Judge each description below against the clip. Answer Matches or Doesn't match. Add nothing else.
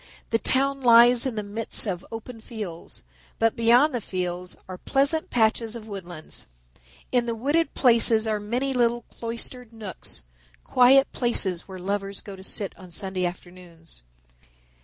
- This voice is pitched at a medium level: Doesn't match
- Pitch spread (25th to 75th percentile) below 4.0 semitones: Doesn't match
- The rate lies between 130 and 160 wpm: Matches